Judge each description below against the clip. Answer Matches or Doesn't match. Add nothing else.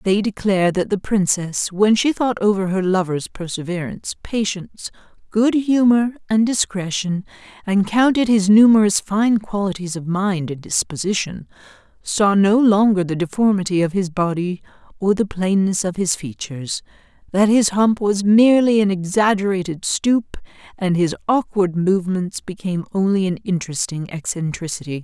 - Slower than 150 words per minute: Matches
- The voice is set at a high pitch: Matches